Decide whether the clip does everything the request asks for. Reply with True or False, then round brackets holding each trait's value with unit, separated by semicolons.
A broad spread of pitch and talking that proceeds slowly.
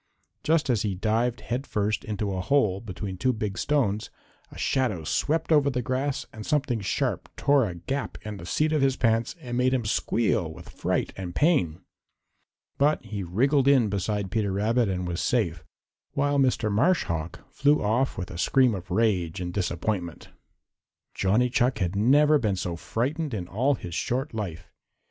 False (5.9 semitones; 175 wpm)